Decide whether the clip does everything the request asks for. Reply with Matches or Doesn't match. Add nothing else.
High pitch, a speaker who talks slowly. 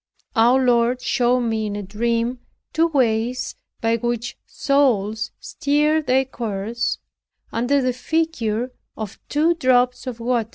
Matches